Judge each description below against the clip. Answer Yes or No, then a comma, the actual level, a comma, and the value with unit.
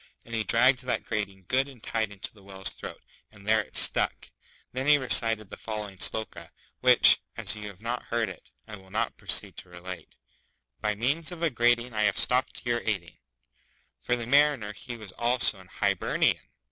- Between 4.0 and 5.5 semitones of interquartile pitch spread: No, average, 3.6 semitones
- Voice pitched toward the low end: Yes, low, 110 Hz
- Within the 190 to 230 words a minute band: Yes, average, 200 wpm